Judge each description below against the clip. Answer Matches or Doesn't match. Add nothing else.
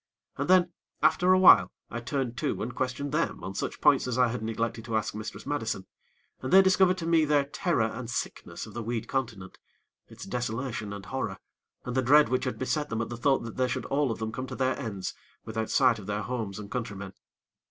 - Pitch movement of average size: Matches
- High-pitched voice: Doesn't match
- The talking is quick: Matches